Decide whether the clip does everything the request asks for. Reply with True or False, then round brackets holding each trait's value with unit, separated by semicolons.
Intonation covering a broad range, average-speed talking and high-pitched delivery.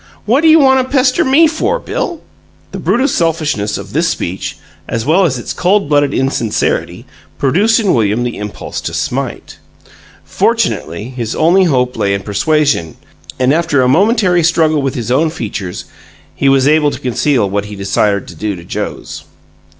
False (8.6 semitones; 170 wpm; 145 Hz)